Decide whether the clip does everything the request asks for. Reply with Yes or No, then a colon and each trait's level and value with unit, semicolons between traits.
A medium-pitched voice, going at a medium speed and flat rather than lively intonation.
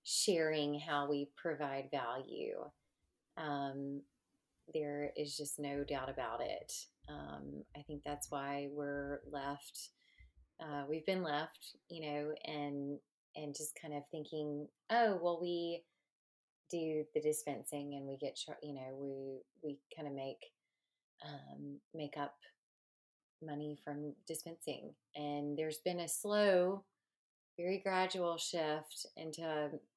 No: medium, 150 Hz; slow, 130 wpm; narrow, 2.2 semitones